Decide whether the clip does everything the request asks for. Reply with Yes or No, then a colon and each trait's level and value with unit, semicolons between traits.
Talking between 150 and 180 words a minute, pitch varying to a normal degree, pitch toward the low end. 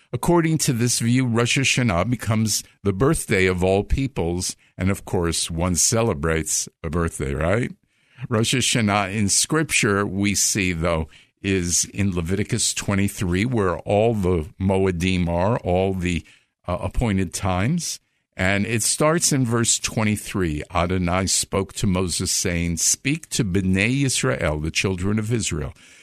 No: average, 140 wpm; average, 4.9 semitones; low, 100 Hz